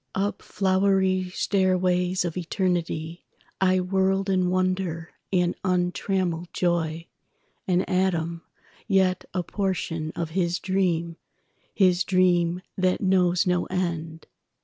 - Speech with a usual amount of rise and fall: No, narrow, 1.6 semitones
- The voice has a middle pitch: Yes, medium, 180 Hz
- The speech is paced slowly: Yes, slow, 95 wpm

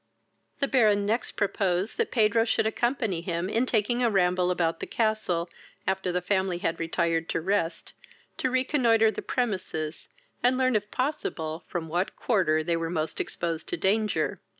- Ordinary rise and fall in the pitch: Yes, average, 4.9 semitones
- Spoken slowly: No, average, 165 wpm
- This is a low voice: No, high, 195 Hz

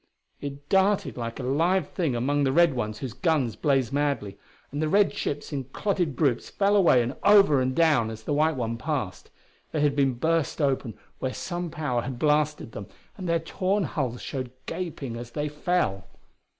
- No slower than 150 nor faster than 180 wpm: No, average, 190 wpm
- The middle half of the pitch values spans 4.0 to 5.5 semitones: Yes, average, 4.8 semitones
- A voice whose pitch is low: No, medium, 145 Hz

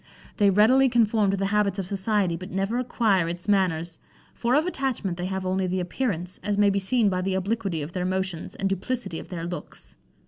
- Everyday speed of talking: No, fast, 210 wpm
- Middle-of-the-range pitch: No, high, 195 Hz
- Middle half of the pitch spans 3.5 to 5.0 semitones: No, average, 2.8 semitones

